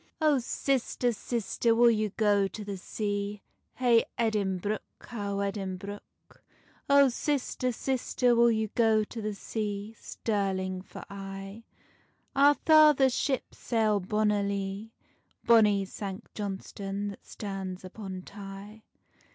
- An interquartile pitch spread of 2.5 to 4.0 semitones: Yes, average, 3.0 semitones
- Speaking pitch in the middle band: No, high, 210 Hz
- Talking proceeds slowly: Yes, slow, 115 wpm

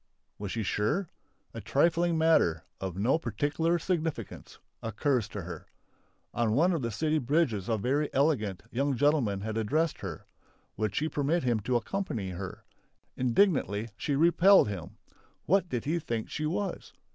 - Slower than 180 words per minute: Yes, average, 155 wpm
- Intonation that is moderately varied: No, wide, 7.2 semitones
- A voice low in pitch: Yes, low, 130 Hz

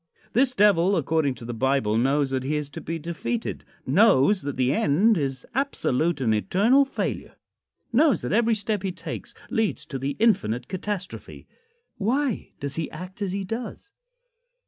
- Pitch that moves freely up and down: Yes, wide, 8.0 semitones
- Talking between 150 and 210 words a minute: Yes, average, 165 wpm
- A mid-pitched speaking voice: Yes, medium, 175 Hz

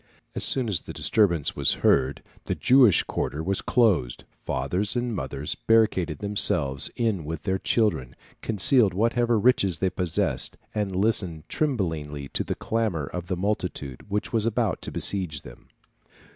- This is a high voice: No, very low, 95 Hz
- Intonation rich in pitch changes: Yes, wide, 6.3 semitones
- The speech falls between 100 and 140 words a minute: No, average, 150 wpm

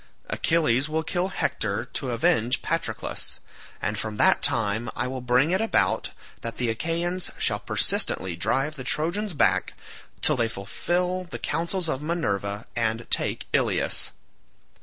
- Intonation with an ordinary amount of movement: No, wide, 7.0 semitones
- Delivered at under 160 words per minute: Yes, average, 140 wpm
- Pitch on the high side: No, low, 125 Hz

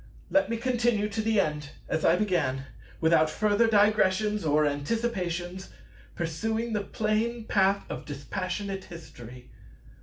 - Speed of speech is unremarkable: No, slow, 125 wpm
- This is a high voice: Yes, high, 195 Hz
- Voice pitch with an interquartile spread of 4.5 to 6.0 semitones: Yes, wide, 5.4 semitones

